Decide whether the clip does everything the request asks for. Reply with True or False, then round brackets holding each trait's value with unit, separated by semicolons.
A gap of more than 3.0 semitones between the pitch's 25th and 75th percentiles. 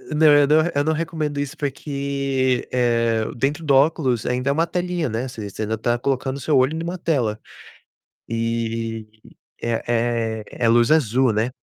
True (4.2 semitones)